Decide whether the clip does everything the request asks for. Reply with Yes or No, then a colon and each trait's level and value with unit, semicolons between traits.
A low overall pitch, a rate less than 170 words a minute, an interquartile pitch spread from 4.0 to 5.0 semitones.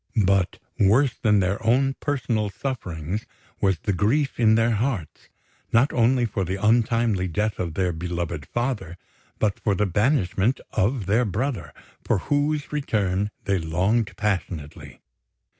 Yes: low, 105 Hz; average, 140 wpm; average, 4.4 semitones